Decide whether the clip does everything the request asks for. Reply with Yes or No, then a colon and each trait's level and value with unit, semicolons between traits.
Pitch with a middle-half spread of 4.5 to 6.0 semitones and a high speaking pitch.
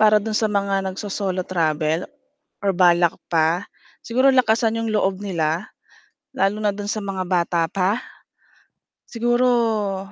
No: average, 3.2 semitones; high, 200 Hz